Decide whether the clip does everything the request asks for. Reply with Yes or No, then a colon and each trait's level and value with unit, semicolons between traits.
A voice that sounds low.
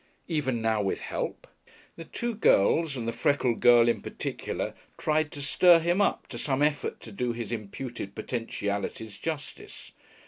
Yes: low, 125 Hz